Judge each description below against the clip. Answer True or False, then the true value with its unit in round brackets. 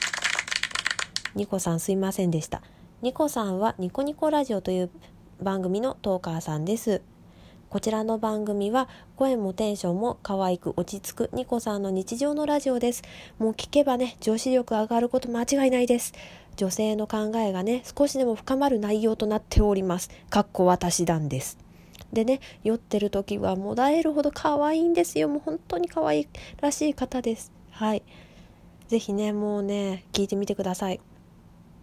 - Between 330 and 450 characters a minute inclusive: True (335 characters per minute)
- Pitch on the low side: False (215 Hz)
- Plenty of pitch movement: False (4.7 semitones)